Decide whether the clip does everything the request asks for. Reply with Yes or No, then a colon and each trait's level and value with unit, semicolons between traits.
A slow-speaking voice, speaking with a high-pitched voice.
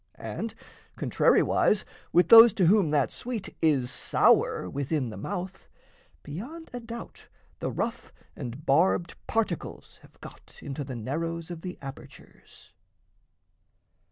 No: slow, 125 wpm; medium, 170 Hz